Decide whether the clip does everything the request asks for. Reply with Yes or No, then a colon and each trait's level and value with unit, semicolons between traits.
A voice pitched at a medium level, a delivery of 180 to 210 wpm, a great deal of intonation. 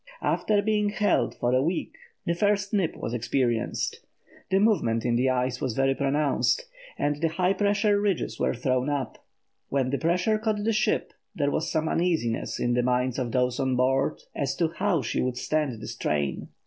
Yes: medium, 145 Hz; average, 185 wpm; wide, 7.2 semitones